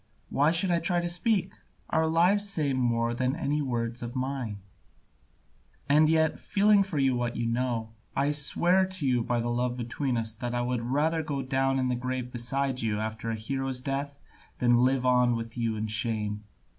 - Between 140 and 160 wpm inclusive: No, average, 195 wpm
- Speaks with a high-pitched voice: No, low, 130 Hz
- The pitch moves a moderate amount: Yes, average, 4.0 semitones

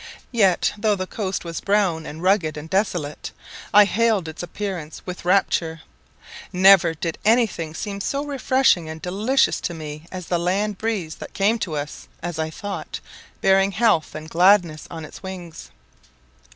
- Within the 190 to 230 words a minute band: No, average, 165 wpm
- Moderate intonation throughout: Yes, average, 4.1 semitones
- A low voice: No, medium, 185 Hz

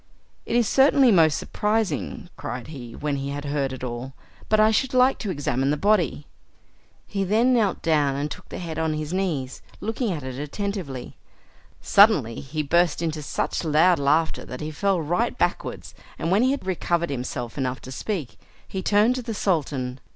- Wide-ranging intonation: Yes, wide, 6.6 semitones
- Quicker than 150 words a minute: Yes, average, 185 wpm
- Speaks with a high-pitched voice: No, medium, 160 Hz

